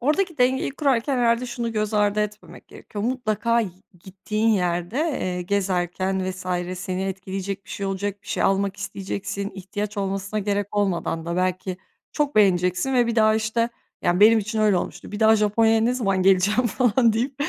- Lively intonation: No, average, 3.2 semitones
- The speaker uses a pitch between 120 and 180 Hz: No, high, 205 Hz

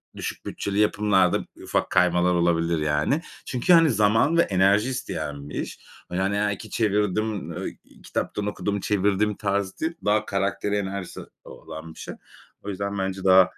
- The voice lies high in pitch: No, low, 100 Hz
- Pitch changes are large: No, narrow, 2.6 semitones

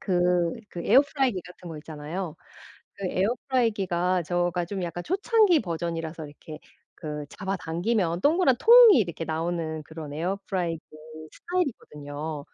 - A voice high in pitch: No, medium, 175 Hz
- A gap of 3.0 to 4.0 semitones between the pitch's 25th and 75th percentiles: No, wide, 5.5 semitones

